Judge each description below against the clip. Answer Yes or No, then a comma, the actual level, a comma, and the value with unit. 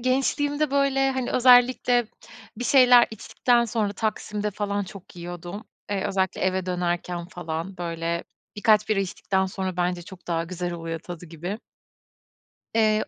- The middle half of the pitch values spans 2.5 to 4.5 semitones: No, average, 5.2 semitones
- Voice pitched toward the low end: No, high, 195 Hz